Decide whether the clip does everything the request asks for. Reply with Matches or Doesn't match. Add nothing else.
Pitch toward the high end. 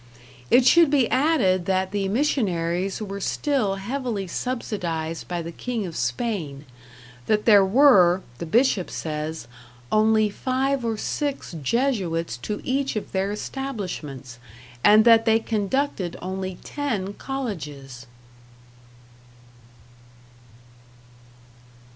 Matches